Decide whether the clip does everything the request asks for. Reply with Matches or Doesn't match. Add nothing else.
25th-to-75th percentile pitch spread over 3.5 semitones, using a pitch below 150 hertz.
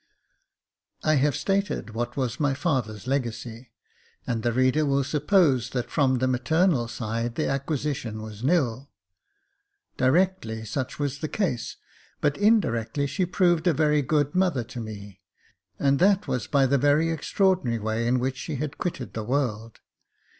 Matches